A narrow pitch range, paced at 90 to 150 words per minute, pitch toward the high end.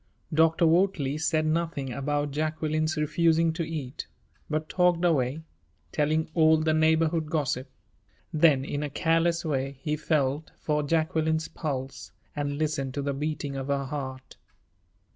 No: narrow, 2.2 semitones; average, 140 wpm; medium, 155 Hz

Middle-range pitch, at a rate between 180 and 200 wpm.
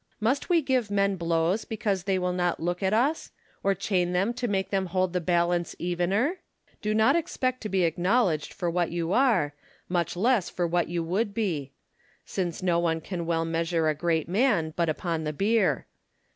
Yes: medium, 180 Hz; average, 190 wpm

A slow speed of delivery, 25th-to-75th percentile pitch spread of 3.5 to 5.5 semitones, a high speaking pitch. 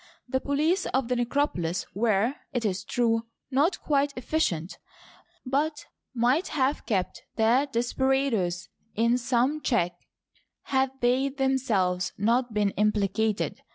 Yes: slow, 120 wpm; average, 4.3 semitones; high, 245 Hz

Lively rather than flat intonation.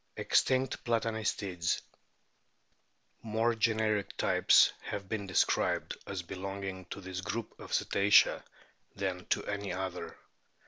No: average, 2.9 semitones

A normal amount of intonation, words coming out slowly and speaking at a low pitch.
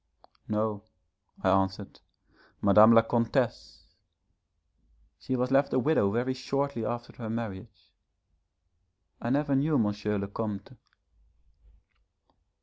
Yes: average, 3.9 semitones; slow, 105 wpm; low, 115 Hz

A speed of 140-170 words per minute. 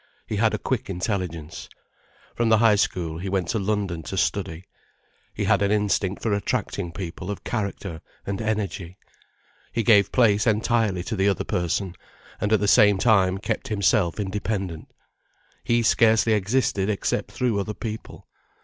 Yes: average, 160 wpm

